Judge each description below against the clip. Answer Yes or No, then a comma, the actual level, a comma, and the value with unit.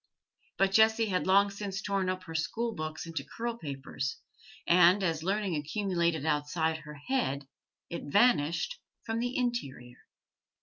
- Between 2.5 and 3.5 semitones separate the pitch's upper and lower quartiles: No, average, 5.3 semitones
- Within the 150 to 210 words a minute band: No, average, 140 wpm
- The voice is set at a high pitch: No, medium, 180 Hz